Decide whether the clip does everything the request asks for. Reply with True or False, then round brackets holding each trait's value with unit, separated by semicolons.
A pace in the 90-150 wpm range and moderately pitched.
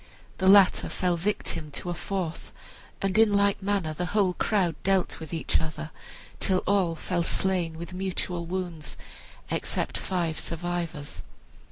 True (145 wpm; 180 Hz)